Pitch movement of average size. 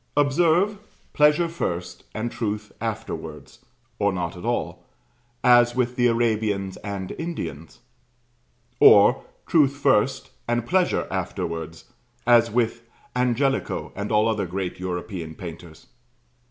No: wide, 5.7 semitones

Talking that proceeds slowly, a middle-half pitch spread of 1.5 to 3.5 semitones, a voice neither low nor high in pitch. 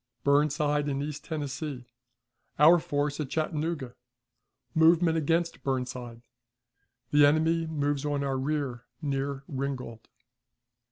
Yes: slow, 105 wpm; narrow, 2.4 semitones; medium, 145 Hz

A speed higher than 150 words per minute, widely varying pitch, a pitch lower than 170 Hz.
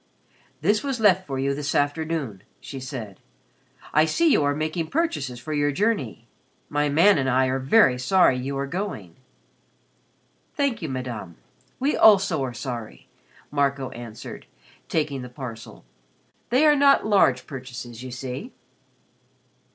No: average, 145 wpm; wide, 6.7 semitones; medium, 140 Hz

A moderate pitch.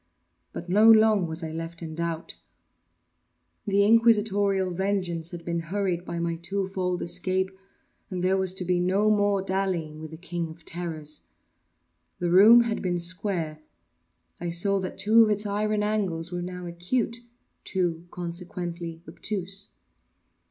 Yes: medium, 180 Hz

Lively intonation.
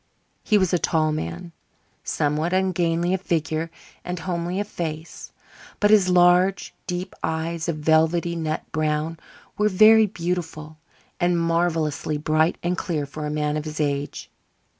No: narrow, 2.5 semitones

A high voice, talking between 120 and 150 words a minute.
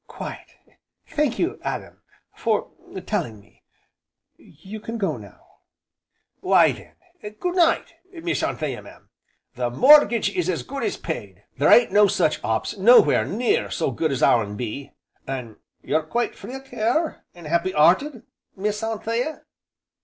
Yes: high, 210 Hz; average, 145 wpm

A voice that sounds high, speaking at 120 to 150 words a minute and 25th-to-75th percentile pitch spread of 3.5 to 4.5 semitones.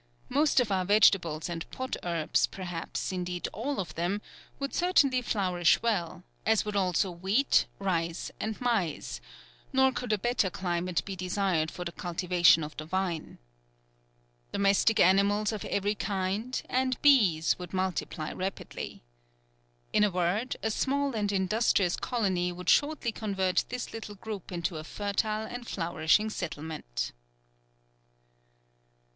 Yes: high, 195 Hz; slow, 135 wpm; average, 3.9 semitones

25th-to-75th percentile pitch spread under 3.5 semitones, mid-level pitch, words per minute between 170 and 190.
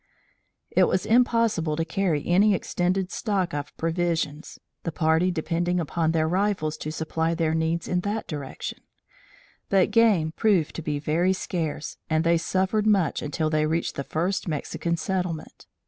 No: average, 2.9 semitones; medium, 170 Hz; average, 155 wpm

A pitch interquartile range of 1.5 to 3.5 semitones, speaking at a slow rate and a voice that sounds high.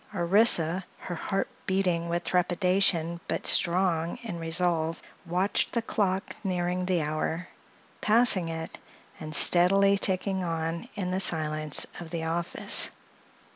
No: narrow, 2.4 semitones; slow, 125 wpm; medium, 175 Hz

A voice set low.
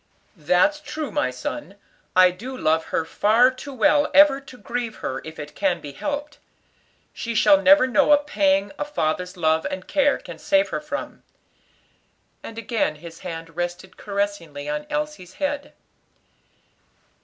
No: high, 225 Hz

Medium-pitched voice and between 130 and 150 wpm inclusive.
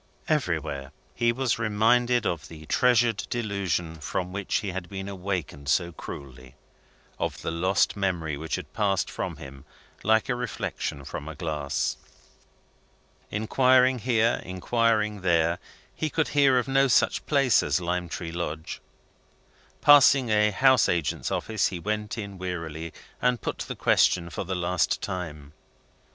No: very low, 95 Hz; average, 145 wpm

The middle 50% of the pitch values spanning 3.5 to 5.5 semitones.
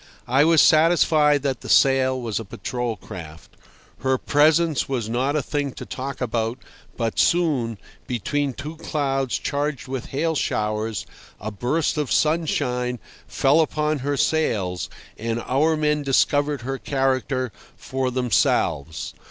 Yes: average, 3.8 semitones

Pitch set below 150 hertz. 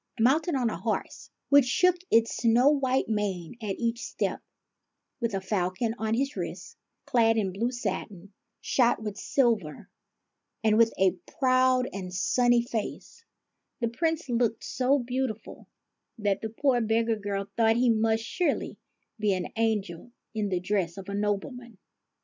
No: high, 225 Hz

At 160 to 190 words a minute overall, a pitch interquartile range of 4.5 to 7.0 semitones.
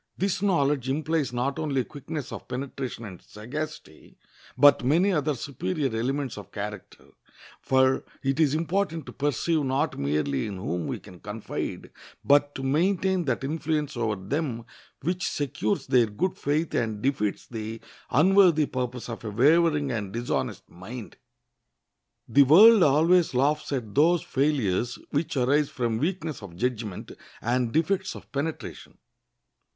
No: average, 140 wpm; average, 4.9 semitones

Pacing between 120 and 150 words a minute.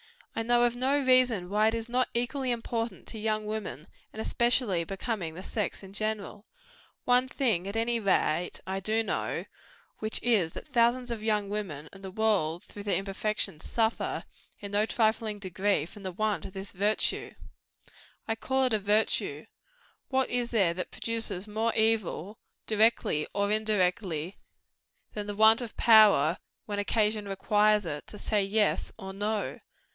No: average, 165 wpm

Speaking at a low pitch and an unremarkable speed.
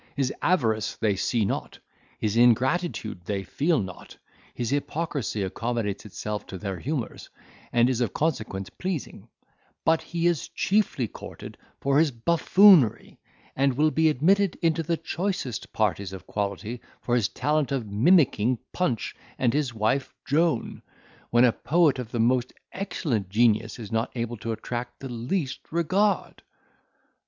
Yes: low, 125 Hz; average, 145 wpm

